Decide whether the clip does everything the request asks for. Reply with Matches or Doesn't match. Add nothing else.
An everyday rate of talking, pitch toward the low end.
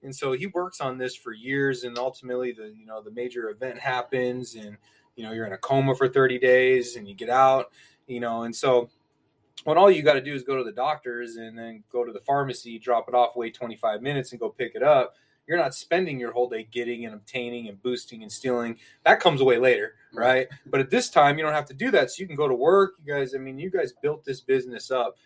Doesn't match